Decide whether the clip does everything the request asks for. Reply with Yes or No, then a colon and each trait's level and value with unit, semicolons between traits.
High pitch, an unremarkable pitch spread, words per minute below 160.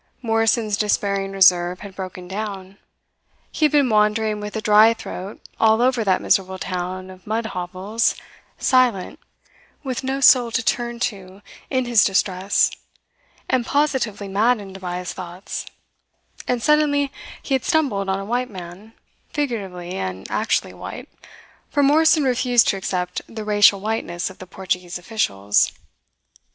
Yes: high, 210 Hz; average, 4.3 semitones; average, 140 wpm